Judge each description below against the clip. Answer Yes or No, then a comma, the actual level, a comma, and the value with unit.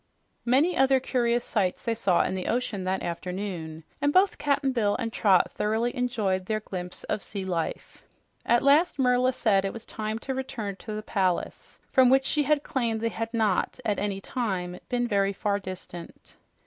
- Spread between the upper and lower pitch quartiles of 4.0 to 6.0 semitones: Yes, average, 4.5 semitones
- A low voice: No, high, 220 Hz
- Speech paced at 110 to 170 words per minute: No, average, 180 wpm